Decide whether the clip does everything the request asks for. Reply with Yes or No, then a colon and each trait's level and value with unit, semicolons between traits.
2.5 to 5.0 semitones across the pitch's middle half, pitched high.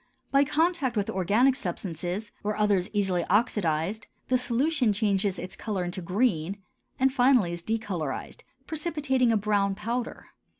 No: wide, 5.4 semitones; high, 210 Hz